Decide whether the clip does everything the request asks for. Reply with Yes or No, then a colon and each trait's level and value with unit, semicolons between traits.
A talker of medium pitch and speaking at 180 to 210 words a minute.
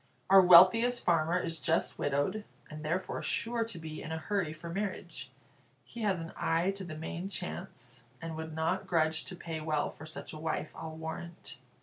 Yes: medium, 165 Hz; average, 190 wpm